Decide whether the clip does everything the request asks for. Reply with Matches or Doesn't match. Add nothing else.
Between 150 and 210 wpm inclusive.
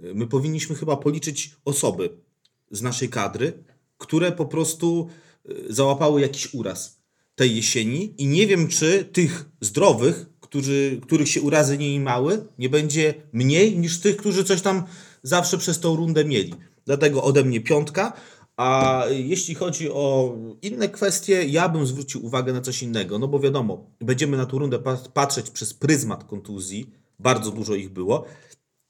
Matches